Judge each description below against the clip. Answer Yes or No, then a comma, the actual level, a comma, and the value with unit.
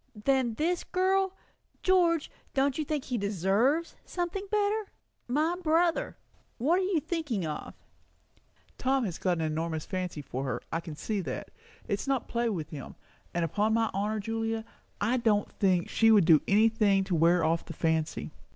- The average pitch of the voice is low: No, high, 225 Hz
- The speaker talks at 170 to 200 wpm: Yes, average, 175 wpm